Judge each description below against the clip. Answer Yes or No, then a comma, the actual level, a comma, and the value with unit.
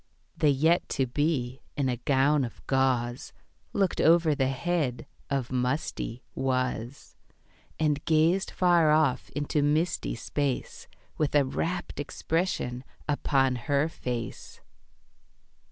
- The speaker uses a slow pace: Yes, slow, 115 wpm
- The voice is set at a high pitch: No, medium, 140 Hz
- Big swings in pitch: No, average, 3.5 semitones